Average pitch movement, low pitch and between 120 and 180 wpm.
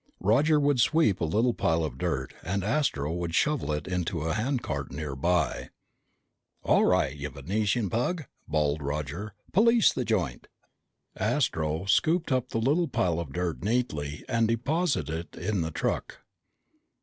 No: wide, 8.3 semitones; very low, 95 Hz; average, 150 wpm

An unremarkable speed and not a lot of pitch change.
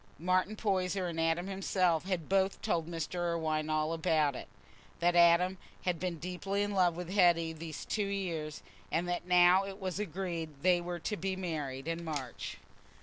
Yes: average, 170 wpm; narrow, 2.3 semitones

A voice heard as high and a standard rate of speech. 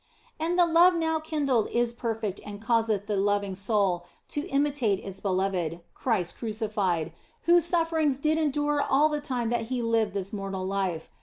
Yes: high, 230 Hz; average, 165 wpm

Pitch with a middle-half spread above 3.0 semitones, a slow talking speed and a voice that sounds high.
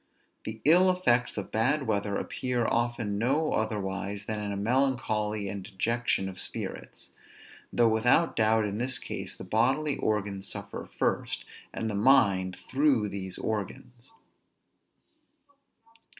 No: average, 3.6 semitones; slow, 130 wpm; low, 110 Hz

